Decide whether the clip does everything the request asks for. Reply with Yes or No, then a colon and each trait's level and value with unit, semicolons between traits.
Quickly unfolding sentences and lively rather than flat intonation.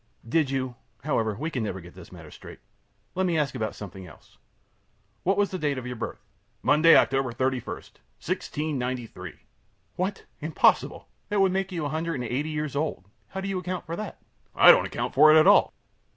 Yes: fast, 210 wpm; wide, 5.8 semitones